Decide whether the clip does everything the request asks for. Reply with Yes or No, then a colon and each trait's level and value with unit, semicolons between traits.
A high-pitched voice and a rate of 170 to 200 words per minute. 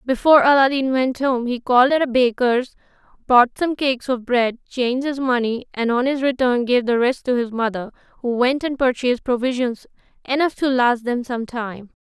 Yes: very high, 250 Hz; average, 190 wpm